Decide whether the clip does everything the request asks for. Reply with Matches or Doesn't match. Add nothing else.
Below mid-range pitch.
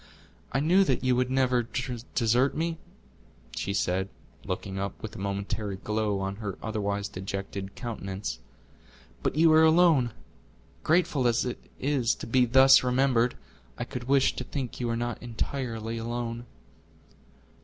Matches